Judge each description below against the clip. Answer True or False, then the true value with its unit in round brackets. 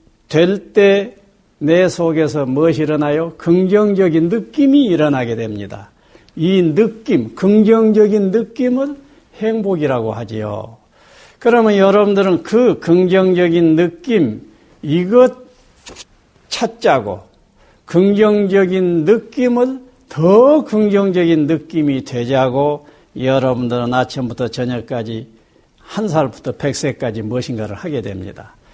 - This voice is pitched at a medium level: True (170 Hz)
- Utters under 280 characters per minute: True (240 characters per minute)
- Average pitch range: False (8.0 semitones)